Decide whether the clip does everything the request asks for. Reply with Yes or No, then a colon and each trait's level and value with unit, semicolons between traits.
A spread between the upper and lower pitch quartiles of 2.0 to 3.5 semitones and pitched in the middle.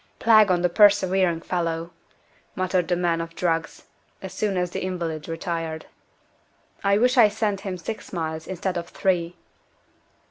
Yes: average, 2.7 semitones; medium, 180 Hz